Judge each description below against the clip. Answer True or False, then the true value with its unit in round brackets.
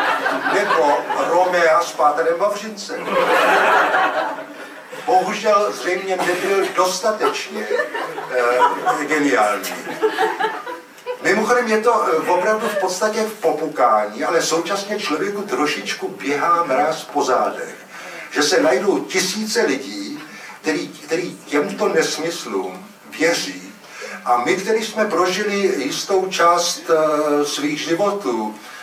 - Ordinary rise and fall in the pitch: True (4.8 semitones)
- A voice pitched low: False (195 Hz)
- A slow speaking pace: True (100 wpm)